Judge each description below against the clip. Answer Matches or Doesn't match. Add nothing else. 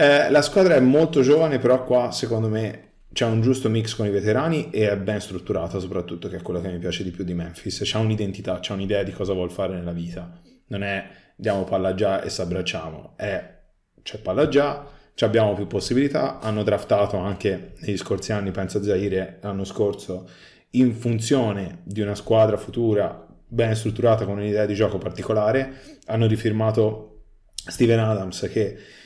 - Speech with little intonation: Doesn't match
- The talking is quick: Matches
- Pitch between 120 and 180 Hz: Doesn't match